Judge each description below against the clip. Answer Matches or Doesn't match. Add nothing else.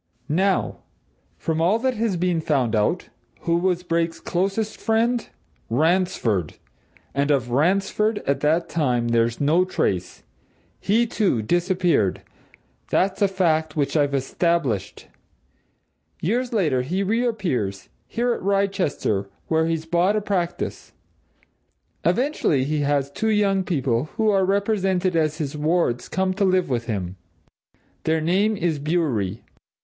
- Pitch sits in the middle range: Matches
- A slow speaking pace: Matches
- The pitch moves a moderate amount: Doesn't match